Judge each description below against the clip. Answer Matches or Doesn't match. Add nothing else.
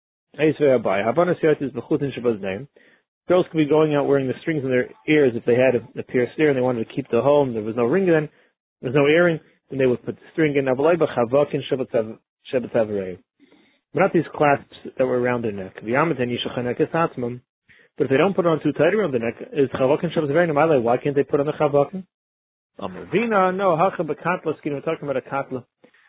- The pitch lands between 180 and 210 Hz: Doesn't match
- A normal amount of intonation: Matches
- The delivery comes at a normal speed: Matches